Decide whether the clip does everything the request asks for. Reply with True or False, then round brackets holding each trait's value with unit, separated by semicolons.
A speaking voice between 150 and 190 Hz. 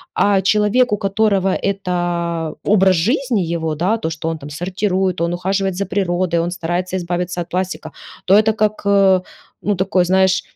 True (185 Hz)